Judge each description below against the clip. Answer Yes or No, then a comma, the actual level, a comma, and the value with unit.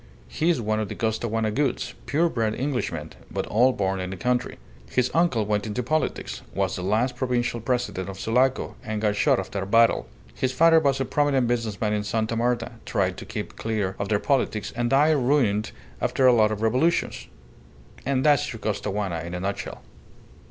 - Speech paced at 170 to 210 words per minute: Yes, average, 190 wpm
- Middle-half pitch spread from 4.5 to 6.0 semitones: No, average, 3.8 semitones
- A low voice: Yes, low, 115 Hz